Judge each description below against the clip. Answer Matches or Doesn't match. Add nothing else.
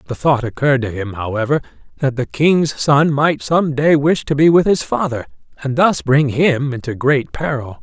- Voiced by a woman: Doesn't match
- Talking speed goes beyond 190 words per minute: Matches